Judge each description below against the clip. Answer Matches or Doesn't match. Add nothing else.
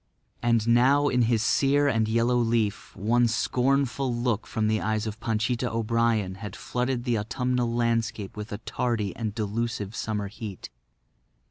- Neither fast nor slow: Matches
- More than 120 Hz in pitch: Doesn't match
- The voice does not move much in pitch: Matches